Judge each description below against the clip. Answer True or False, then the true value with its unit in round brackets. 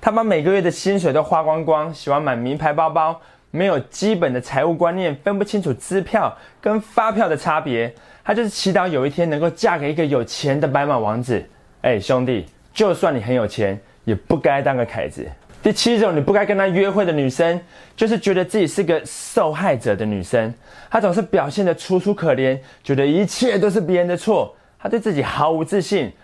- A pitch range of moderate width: False (6.9 semitones)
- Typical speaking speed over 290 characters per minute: True (300 characters per minute)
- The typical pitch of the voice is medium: True (165 Hz)